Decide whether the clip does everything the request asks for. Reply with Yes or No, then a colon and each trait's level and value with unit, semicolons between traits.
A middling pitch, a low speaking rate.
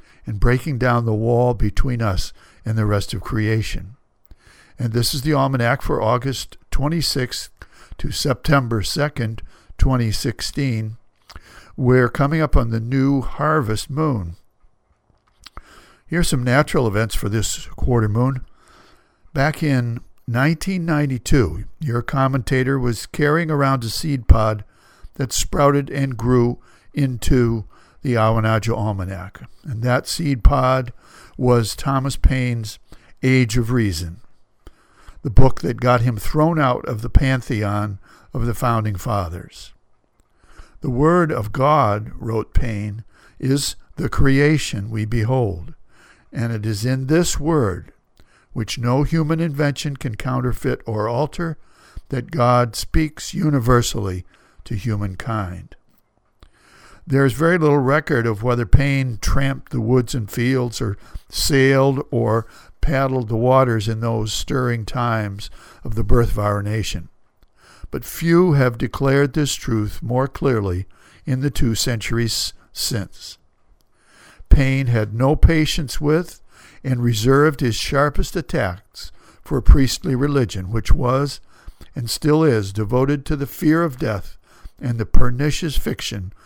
No: low, 125 Hz; slow, 130 wpm